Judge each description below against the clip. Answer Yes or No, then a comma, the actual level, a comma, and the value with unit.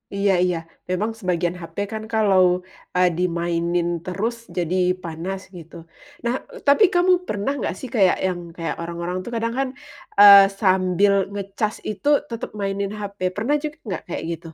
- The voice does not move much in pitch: No, average, 3.2 semitones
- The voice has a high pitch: Yes, high, 195 Hz